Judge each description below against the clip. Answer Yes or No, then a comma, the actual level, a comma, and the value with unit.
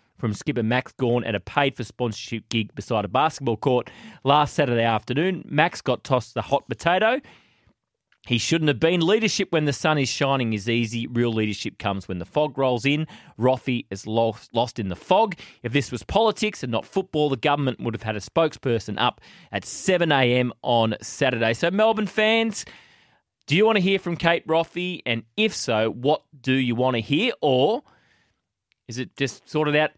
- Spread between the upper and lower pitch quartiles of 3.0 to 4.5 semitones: No, average, 5.2 semitones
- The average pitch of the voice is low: Yes, low, 130 Hz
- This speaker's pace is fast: No, average, 190 wpm